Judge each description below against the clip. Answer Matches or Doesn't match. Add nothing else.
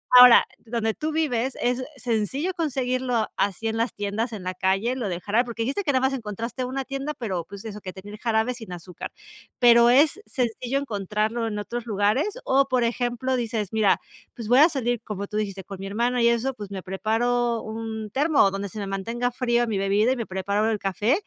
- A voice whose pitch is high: Matches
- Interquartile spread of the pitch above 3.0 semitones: Matches